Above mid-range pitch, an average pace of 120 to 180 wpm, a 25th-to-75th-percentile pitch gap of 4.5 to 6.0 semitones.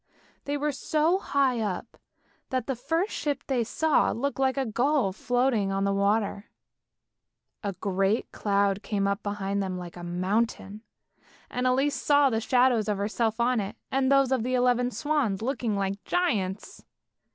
Yes: high, 235 Hz; average, 165 wpm; average, 5.1 semitones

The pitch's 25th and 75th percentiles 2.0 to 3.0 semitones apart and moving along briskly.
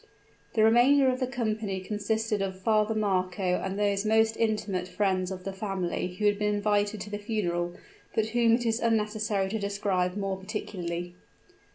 No: narrow, 2.6 semitones; average, 170 wpm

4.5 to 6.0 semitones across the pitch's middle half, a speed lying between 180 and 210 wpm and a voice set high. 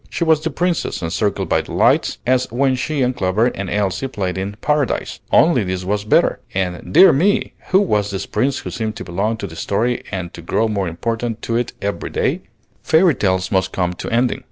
No: wide, 5.5 semitones; fast, 205 wpm; low, 110 Hz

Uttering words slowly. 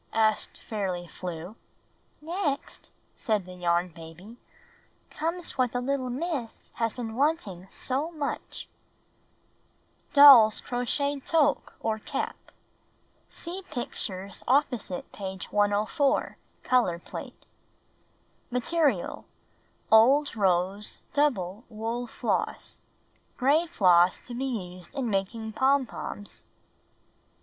Yes: slow, 100 wpm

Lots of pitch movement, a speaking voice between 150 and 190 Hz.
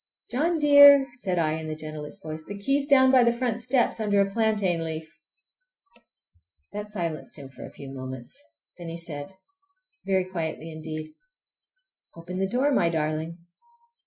Yes: wide, 7.8 semitones; medium, 185 Hz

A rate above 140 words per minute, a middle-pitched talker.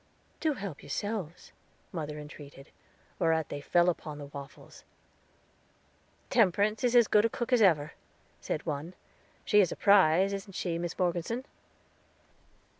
No: slow, 135 wpm; medium, 175 Hz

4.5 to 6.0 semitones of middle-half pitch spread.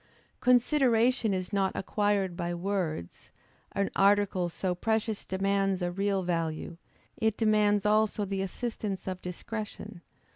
No: narrow, 2.6 semitones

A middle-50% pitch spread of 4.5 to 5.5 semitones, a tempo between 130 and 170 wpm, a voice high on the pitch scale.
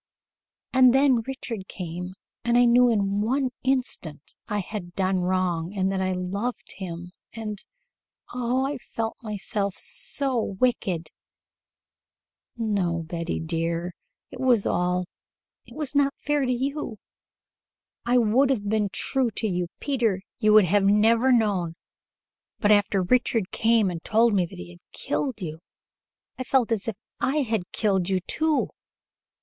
Yes: average, 5.2 semitones; average, 150 wpm; high, 210 Hz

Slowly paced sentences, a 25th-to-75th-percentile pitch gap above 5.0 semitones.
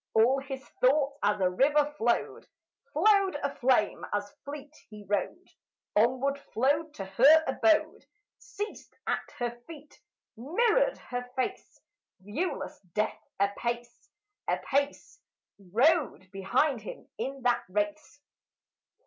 Yes: slow, 110 wpm; wide, 5.5 semitones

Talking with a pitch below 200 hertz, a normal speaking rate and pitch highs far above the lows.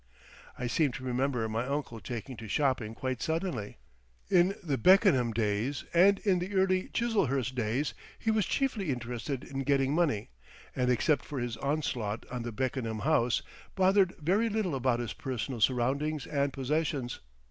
Yes: low, 135 Hz; average, 160 wpm; wide, 5.7 semitones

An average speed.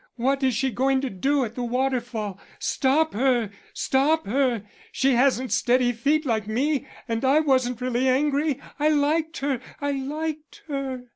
Yes: average, 160 wpm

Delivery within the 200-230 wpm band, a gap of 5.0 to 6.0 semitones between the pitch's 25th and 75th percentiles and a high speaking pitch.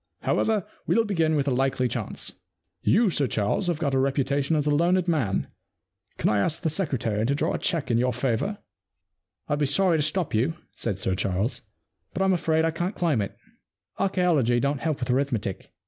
No: fast, 205 wpm; wide, 5.4 semitones; medium, 145 Hz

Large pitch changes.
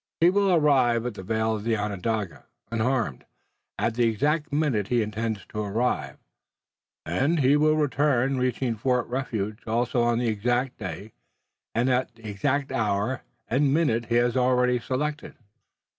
No: average, 3.4 semitones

